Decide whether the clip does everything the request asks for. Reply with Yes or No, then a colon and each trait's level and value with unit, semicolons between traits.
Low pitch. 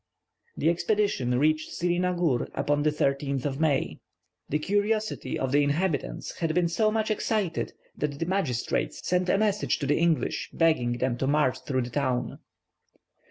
No: medium, 155 Hz